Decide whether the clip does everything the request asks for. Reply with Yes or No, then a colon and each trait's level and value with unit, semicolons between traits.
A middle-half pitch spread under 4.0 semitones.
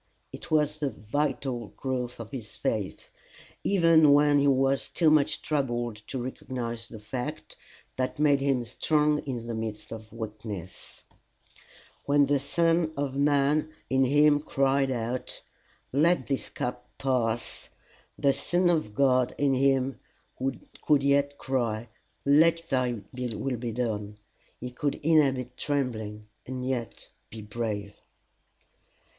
Yes: average, 3.5 semitones